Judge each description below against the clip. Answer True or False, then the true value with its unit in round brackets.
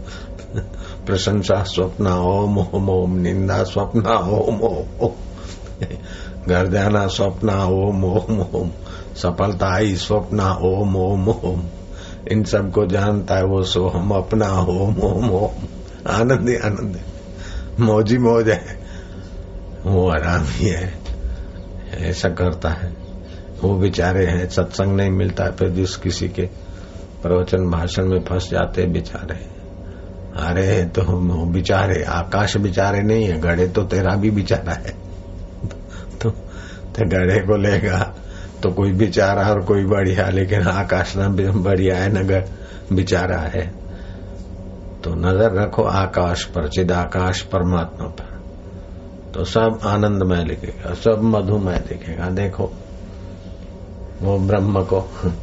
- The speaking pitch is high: False (95 Hz)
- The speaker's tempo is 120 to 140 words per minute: True (130 wpm)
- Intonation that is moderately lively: False (1.3 semitones)